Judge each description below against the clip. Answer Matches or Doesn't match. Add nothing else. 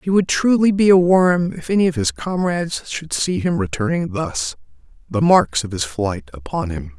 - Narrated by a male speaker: Matches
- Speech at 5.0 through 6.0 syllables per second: Doesn't match